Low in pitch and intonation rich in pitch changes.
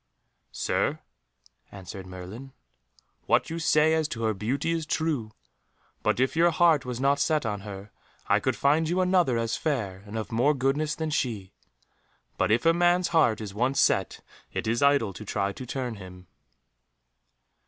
Yes: low, 130 Hz; wide, 6.6 semitones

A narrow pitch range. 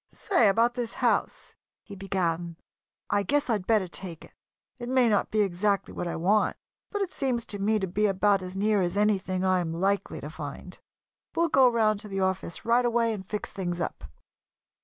No: average, 3.5 semitones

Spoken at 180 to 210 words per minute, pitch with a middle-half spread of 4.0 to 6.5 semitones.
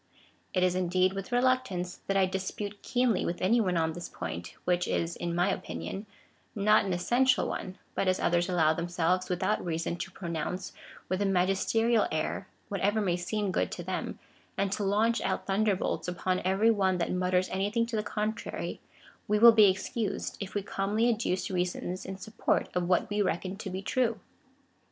No: average, 185 wpm; average, 2.8 semitones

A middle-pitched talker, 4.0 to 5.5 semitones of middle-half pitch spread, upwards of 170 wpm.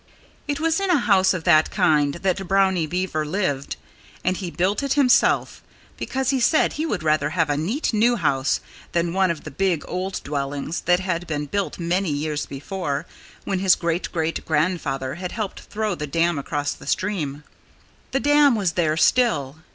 Yes: medium, 175 Hz; average, 4.5 semitones; average, 180 wpm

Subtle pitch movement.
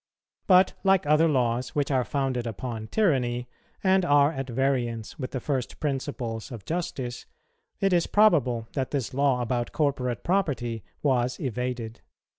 No: average, 3.7 semitones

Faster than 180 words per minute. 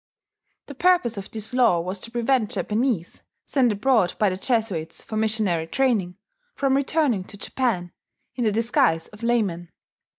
No: average, 155 wpm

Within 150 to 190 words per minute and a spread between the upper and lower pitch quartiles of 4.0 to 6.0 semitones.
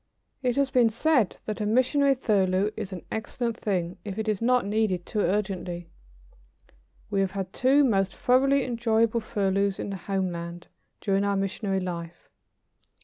No: average, 155 wpm; average, 3.6 semitones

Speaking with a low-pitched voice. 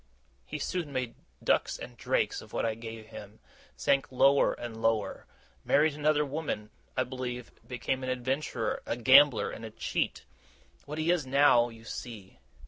Yes: low, 130 Hz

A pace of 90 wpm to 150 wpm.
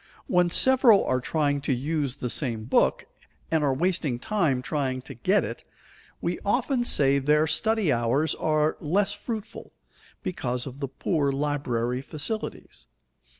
Yes: average, 145 wpm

